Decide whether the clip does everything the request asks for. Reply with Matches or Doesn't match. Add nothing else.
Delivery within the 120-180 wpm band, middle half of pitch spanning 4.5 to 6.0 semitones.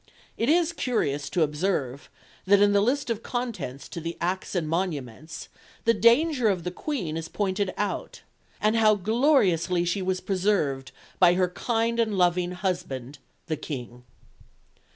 Matches